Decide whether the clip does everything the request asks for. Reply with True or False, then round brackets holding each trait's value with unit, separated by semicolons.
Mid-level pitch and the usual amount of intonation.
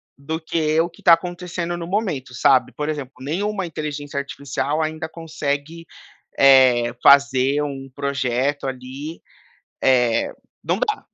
True (145 Hz; 3.5 semitones)